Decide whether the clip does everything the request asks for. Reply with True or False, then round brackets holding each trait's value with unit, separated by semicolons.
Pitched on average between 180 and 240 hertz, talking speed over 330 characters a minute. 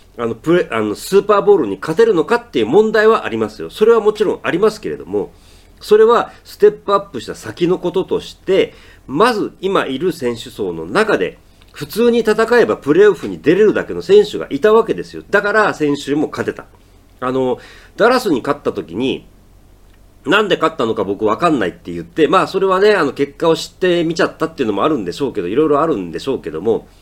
True (185 Hz; 425 characters per minute)